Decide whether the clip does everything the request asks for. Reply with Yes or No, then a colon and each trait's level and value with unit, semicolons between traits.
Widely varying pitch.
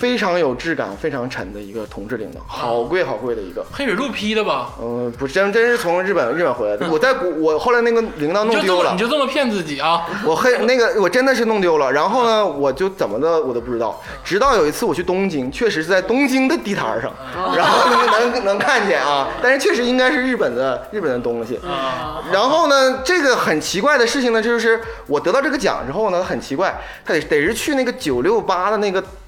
Yes: wide, 7.9 semitones